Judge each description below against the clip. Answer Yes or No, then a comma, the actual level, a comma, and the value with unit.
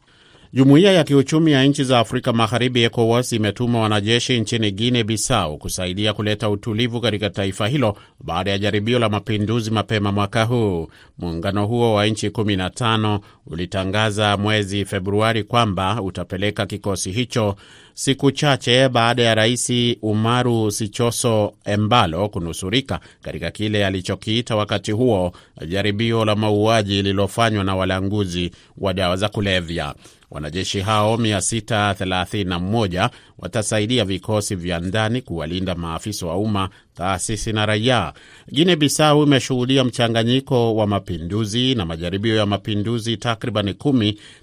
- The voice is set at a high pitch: No, low, 105 Hz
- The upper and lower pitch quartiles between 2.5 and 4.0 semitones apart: Yes, average, 3.1 semitones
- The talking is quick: No, average, 120 wpm